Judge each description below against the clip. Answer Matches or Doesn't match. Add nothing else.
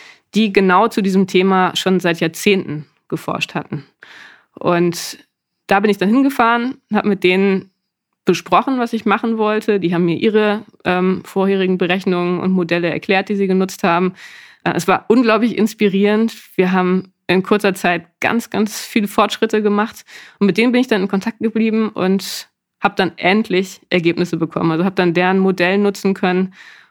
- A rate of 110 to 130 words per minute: Doesn't match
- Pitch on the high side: Matches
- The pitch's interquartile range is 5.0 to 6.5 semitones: Doesn't match